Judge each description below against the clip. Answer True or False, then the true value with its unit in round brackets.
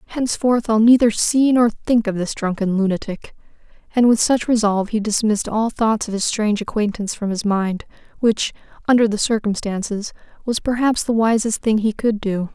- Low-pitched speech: False (220 Hz)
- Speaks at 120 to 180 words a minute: True (175 wpm)